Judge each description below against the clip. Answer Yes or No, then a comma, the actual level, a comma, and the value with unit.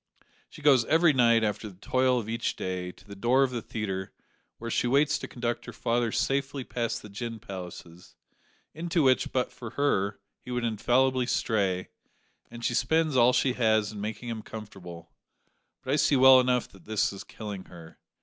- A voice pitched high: No, low, 115 Hz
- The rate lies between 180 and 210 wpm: Yes, average, 190 wpm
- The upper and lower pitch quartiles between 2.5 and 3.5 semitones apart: No, average, 3.9 semitones